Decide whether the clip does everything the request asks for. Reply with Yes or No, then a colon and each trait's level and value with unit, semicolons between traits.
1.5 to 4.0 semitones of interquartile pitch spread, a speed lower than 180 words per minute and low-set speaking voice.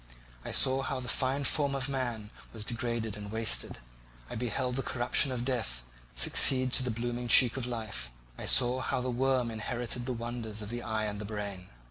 No: average, 2.7 semitones; average, 190 wpm; low, 120 Hz